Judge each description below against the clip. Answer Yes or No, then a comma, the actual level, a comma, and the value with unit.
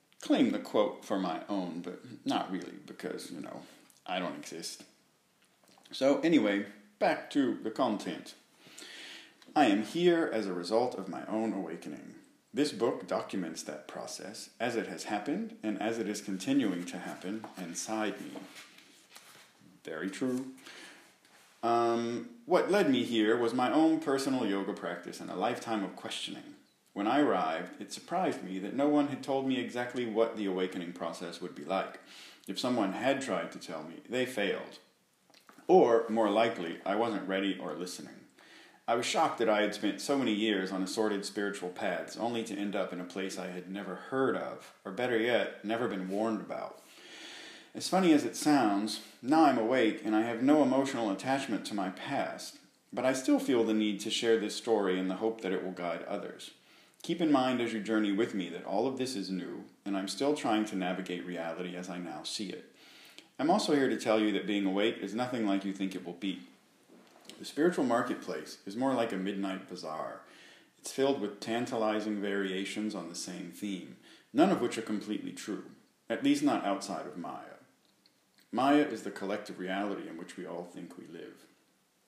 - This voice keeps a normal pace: Yes, average, 190 wpm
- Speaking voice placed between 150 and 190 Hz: No, low, 110 Hz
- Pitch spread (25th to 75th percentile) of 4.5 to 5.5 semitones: Yes, average, 5.0 semitones